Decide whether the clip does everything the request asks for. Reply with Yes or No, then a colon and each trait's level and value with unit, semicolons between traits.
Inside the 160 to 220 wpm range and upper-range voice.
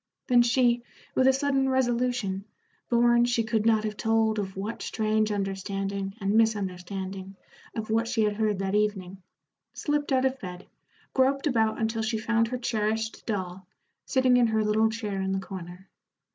Yes: average, 165 wpm; high, 220 Hz